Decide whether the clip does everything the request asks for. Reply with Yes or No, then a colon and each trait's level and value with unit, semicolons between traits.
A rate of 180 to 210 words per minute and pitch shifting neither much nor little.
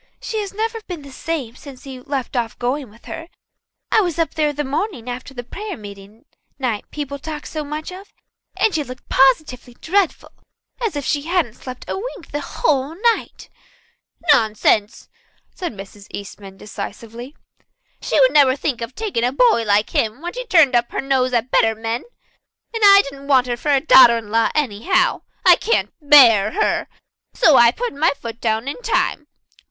No: average, 185 wpm; wide, 5.8 semitones